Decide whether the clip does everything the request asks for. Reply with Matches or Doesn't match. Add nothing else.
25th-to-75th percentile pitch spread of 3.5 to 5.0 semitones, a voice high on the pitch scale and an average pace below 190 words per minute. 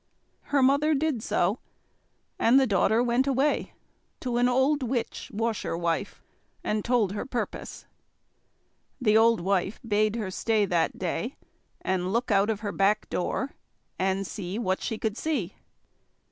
Matches